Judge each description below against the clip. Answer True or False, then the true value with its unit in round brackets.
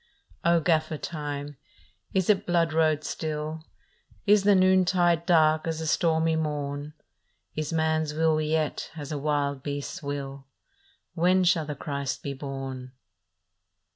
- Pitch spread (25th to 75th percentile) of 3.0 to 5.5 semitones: False (2.4 semitones)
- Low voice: False (155 Hz)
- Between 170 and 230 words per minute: False (145 wpm)